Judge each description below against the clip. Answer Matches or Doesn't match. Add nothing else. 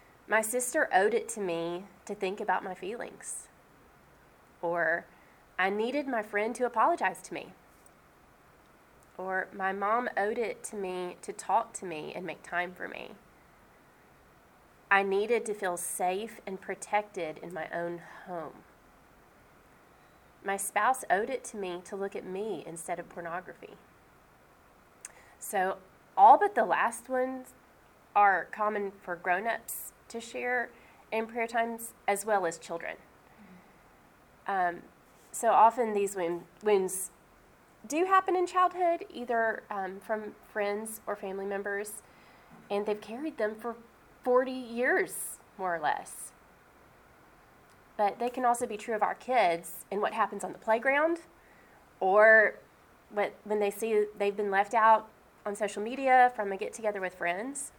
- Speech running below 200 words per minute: Matches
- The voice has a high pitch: Matches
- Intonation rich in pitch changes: Doesn't match